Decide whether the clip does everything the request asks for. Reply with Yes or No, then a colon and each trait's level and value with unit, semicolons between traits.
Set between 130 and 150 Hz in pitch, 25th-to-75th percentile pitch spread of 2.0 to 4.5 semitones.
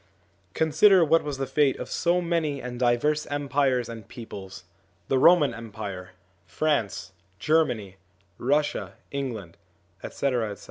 No: low, 135 Hz; wide, 5.5 semitones